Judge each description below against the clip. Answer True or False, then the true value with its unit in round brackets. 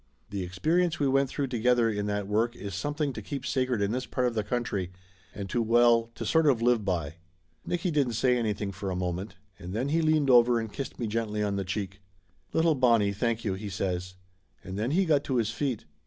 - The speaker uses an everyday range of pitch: True (4.6 semitones)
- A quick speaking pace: True (230 wpm)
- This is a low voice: True (115 Hz)